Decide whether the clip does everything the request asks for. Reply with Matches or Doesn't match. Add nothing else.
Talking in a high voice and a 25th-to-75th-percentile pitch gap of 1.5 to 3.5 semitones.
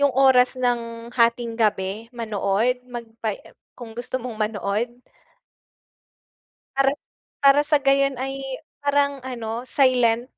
Matches